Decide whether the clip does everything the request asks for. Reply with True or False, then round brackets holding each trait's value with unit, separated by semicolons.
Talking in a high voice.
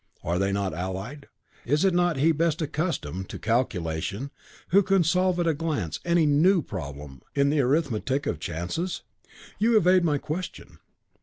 False (145 Hz)